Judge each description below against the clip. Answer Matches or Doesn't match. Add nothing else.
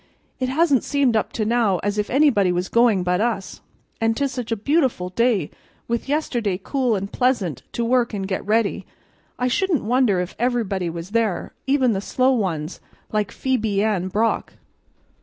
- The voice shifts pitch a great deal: Doesn't match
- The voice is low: Doesn't match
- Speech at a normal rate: Matches